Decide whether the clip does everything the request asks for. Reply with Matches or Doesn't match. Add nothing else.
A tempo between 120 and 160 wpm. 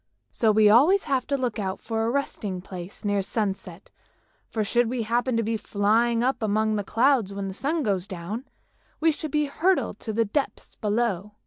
Doesn't match